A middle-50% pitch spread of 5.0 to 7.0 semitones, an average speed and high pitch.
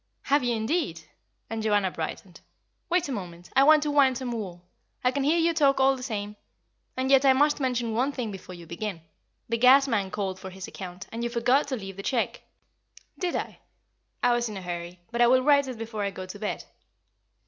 No: wide, 5.6 semitones; fast, 220 wpm; high, 235 Hz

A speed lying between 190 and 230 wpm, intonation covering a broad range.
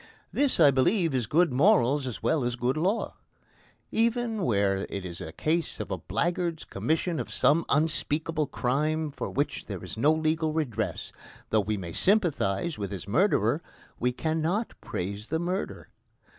No: average, 160 wpm; wide, 6.2 semitones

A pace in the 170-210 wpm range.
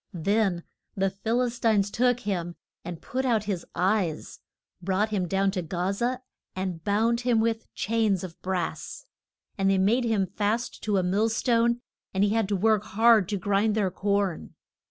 Yes: average, 175 wpm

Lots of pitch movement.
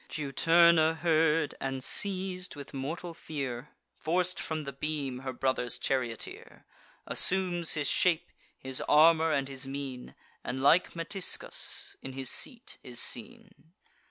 No: average, 4.2 semitones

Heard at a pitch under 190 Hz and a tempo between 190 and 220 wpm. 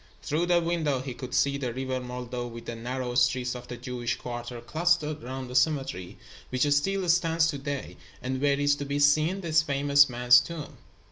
Yes: low, 135 Hz; average, 195 wpm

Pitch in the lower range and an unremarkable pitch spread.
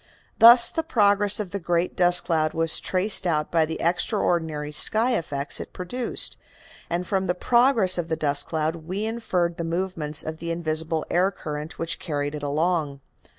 No: medium, 170 Hz; average, 3.4 semitones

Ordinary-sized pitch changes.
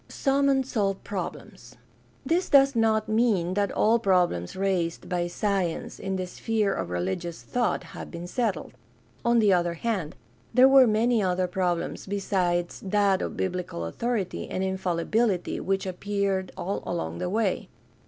Yes: average, 3.9 semitones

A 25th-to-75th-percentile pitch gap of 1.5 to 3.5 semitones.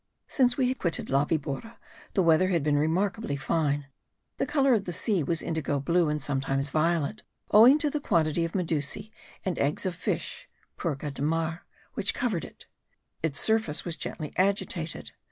No: average, 5.2 semitones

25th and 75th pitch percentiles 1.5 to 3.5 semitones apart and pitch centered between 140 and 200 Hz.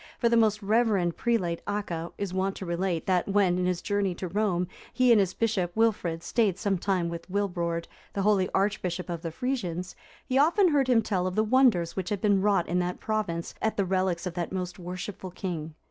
Yes: average, 3.2 semitones; high, 190 Hz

